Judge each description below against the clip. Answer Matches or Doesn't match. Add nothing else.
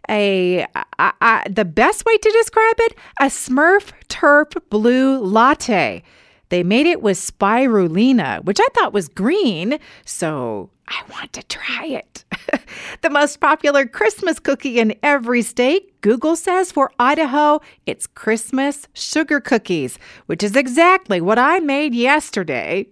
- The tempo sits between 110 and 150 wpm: Matches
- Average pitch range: Doesn't match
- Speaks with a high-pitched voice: Matches